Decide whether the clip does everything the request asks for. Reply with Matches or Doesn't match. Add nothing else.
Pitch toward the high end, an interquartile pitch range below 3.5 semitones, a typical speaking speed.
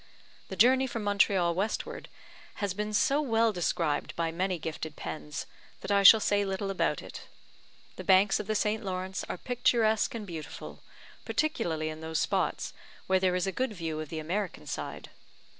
Doesn't match